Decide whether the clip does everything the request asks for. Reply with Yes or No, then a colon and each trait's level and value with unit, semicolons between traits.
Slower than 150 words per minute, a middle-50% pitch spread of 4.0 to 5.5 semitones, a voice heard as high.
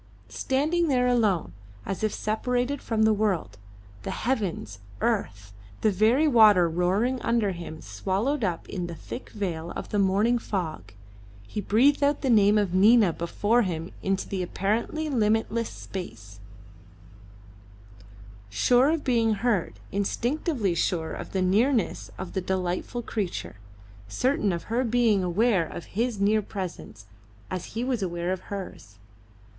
Yes: average, 140 wpm; average, 5.0 semitones; high, 205 Hz